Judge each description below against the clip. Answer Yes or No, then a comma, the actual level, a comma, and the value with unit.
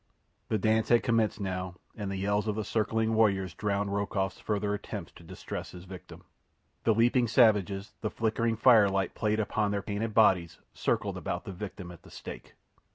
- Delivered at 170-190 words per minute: Yes, average, 175 wpm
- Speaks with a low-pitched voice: Yes, low, 105 Hz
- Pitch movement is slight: Yes, narrow, 2.3 semitones